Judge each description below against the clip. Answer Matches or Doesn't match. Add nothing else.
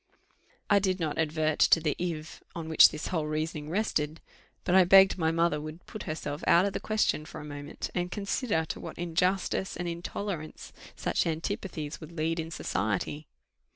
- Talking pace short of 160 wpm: Doesn't match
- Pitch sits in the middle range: Matches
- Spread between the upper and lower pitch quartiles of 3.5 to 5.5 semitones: Doesn't match